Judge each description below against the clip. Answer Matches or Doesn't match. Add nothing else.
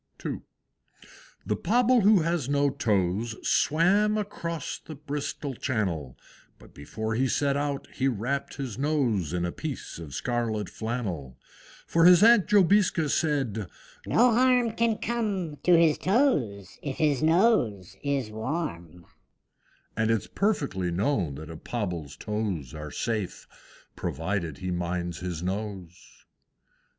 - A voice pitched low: Matches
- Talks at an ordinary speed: Doesn't match